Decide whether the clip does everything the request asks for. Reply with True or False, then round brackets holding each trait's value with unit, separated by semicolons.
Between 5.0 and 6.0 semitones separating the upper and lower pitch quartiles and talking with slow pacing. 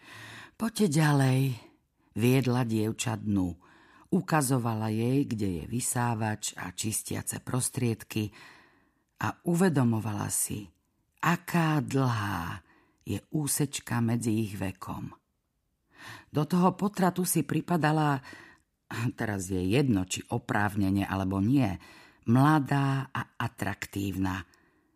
True (5.4 semitones; 90 wpm)